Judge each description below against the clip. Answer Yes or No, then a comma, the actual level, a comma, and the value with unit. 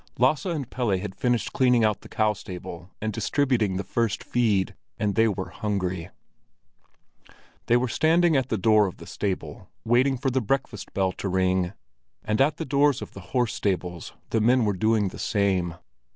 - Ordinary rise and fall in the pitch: Yes, average, 4.8 semitones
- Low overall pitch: Yes, low, 110 Hz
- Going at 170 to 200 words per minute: Yes, average, 180 wpm